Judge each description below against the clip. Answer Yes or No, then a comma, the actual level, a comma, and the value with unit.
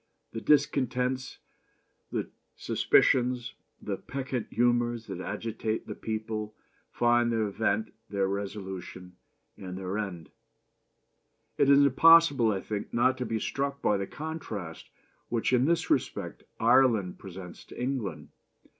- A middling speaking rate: No, slow, 130 wpm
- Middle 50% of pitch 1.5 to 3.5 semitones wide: No, average, 4.4 semitones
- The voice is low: Yes, low, 115 Hz